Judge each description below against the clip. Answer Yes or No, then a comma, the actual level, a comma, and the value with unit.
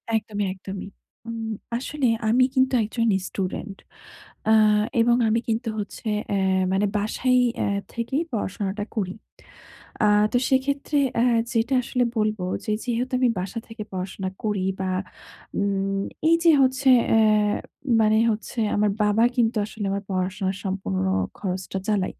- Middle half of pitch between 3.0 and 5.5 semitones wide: Yes, average, 3.7 semitones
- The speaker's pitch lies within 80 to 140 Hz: No, high, 215 Hz